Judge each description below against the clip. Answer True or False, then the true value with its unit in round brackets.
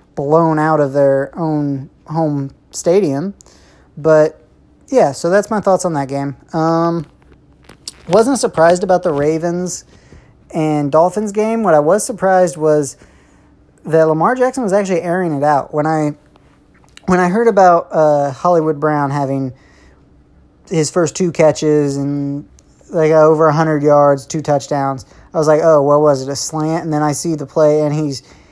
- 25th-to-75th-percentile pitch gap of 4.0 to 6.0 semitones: False (3.2 semitones)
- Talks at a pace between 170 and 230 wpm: False (160 wpm)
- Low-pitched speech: False (155 Hz)